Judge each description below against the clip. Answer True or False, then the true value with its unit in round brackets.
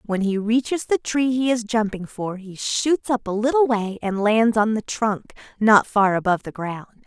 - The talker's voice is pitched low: False (220 Hz)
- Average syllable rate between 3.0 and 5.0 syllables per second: True (4.7 syllables/s)